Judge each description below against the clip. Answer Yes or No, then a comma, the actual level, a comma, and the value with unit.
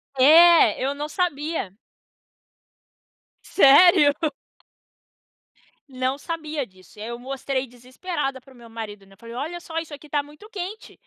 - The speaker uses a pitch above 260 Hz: Yes, very high, 280 Hz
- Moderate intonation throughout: Yes, average, 4.6 semitones